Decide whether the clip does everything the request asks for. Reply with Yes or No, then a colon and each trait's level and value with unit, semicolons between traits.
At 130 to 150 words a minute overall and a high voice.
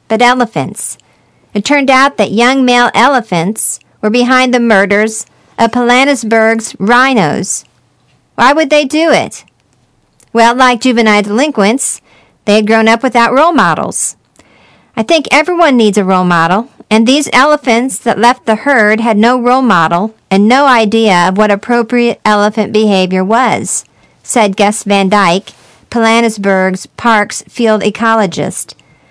Yes: average, 140 wpm; high, 225 Hz